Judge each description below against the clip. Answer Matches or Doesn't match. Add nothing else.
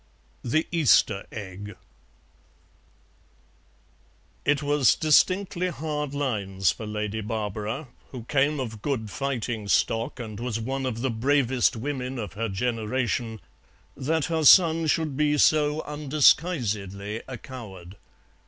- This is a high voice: Doesn't match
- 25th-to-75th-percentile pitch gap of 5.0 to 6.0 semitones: Matches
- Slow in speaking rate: Matches